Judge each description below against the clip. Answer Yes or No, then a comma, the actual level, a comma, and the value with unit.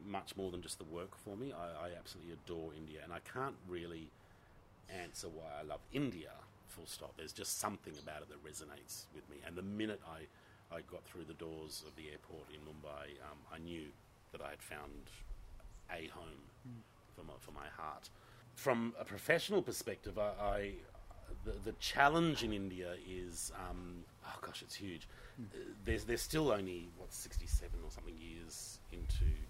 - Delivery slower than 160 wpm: No, average, 185 wpm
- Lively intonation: No, average, 4.9 semitones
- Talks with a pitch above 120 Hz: No, very low, 90 Hz